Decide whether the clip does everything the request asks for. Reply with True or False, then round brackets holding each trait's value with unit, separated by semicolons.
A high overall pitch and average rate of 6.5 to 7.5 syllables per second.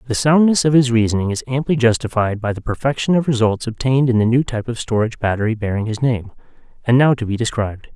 False (120 Hz; 6.6 syllables/s)